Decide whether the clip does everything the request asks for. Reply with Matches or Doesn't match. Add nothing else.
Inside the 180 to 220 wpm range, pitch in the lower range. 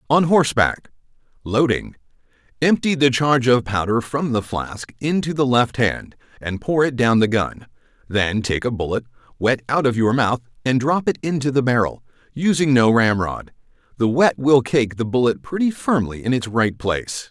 Doesn't match